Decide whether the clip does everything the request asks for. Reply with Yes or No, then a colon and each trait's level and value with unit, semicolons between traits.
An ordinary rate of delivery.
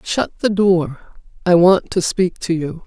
Yes: average, 190 wpm